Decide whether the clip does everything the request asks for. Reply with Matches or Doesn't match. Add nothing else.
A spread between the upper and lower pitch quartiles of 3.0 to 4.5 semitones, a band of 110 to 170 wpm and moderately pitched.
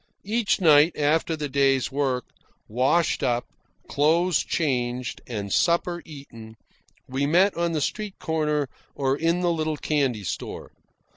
Matches